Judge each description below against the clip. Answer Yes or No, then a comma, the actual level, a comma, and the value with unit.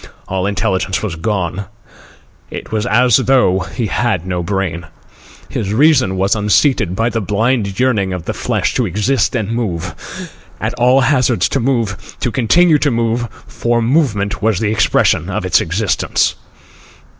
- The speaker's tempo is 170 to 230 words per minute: No, average, 155 wpm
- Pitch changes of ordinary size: Yes, average, 4.2 semitones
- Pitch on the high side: No, low, 110 Hz